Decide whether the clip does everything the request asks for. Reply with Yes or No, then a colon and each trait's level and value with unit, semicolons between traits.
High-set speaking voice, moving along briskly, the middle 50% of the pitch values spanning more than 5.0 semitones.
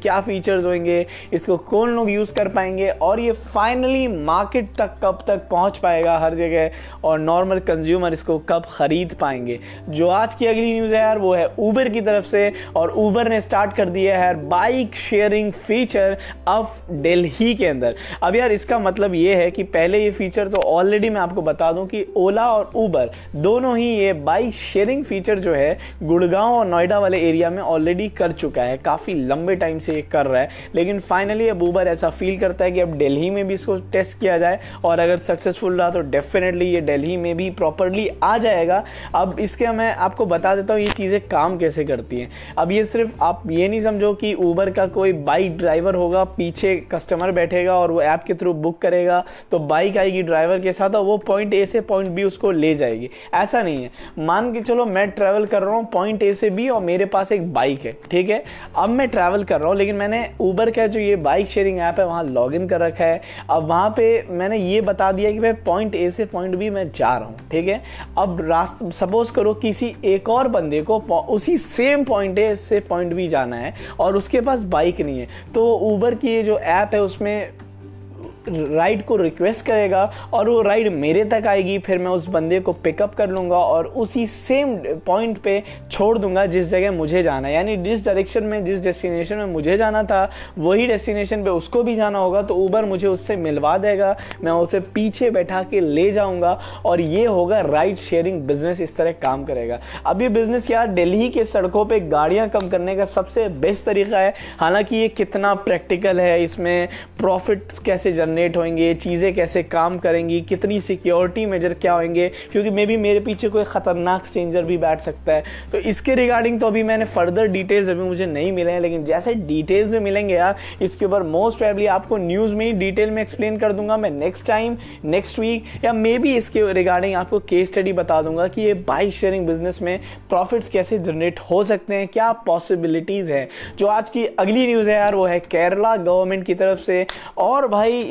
No: high, 195 Hz; fast, 205 wpm; average, 3.5 semitones